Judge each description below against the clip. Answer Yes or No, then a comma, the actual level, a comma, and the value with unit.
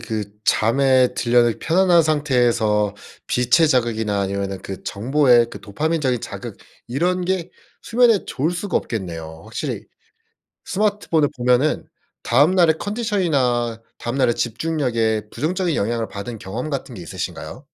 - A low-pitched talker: Yes, low, 125 Hz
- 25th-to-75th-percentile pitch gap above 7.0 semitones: No, wide, 6.3 semitones